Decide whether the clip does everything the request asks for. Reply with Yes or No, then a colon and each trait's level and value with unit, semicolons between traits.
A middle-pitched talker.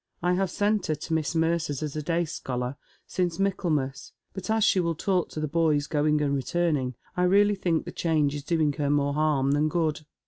Yes: medium, 155 Hz